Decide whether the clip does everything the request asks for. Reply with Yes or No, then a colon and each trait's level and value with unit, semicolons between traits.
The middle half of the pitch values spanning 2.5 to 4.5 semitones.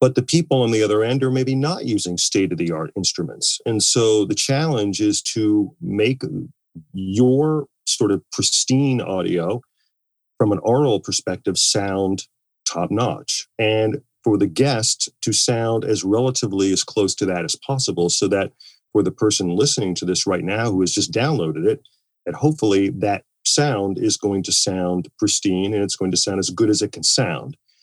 No: average, 5.1 semitones